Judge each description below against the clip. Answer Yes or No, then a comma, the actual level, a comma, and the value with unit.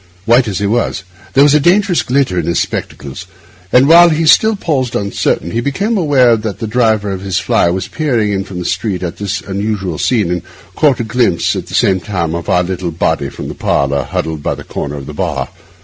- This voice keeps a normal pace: No, fast, 225 wpm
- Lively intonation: Yes, wide, 6.6 semitones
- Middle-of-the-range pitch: No, low, 105 Hz